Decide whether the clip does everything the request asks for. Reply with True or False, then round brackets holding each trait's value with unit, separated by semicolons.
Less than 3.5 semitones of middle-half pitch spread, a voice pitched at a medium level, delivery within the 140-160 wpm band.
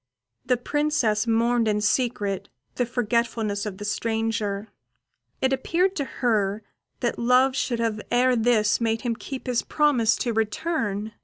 False (2.8 semitones; 230 Hz; 145 wpm)